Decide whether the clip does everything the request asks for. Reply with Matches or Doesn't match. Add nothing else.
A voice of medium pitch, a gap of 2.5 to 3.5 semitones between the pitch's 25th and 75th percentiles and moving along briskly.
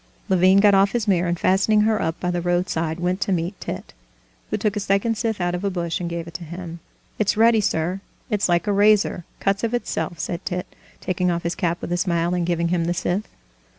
Matches